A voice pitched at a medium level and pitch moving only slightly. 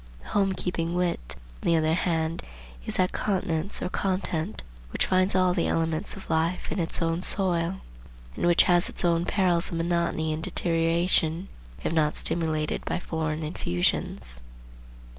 Yes: medium, 170 Hz; narrow, 2.1 semitones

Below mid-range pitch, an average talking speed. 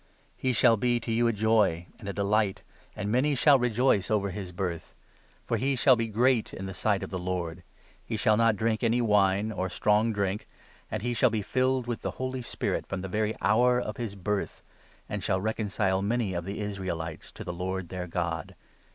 No: low, 105 Hz; fast, 215 wpm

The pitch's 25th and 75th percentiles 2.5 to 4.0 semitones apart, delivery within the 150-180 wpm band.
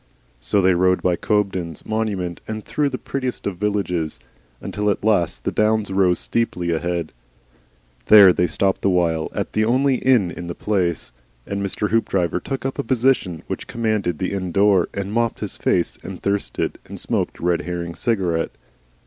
Yes: average, 3.7 semitones; average, 175 wpm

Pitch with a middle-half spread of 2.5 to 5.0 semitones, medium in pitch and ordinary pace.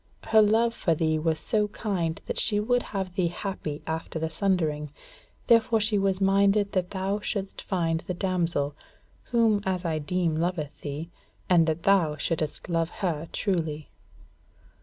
Yes: average, 3.8 semitones; medium, 180 Hz; average, 160 wpm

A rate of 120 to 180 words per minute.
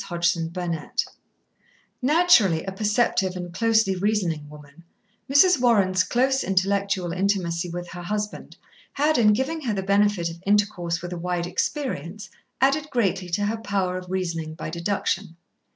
Yes: average, 150 wpm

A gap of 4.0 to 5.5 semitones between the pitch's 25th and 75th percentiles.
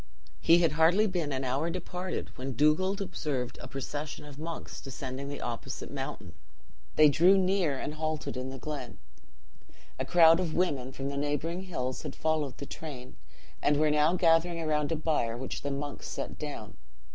No: average, 3.4 semitones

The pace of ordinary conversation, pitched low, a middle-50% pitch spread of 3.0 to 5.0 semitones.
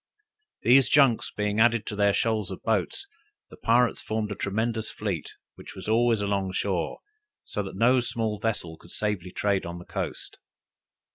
No: average, 165 wpm; low, 105 Hz; narrow, 2.6 semitones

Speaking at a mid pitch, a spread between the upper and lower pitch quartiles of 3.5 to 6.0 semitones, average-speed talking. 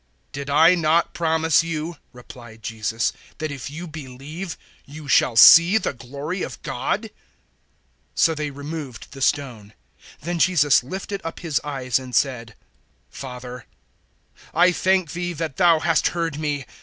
Yes: medium, 150 Hz; average, 4.2 semitones; average, 150 wpm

